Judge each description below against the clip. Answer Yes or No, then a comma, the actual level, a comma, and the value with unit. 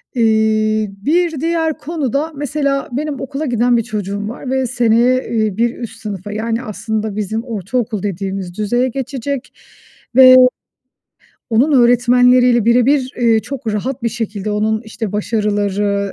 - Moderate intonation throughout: Yes, average, 3.4 semitones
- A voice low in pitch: No, high, 235 Hz